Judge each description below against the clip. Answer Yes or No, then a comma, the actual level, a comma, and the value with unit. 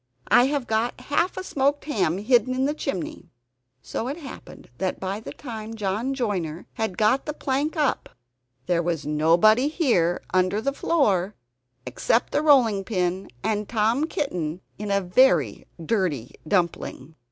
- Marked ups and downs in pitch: Yes, wide, 6.9 semitones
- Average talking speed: Yes, average, 150 wpm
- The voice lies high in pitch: Yes, high, 215 Hz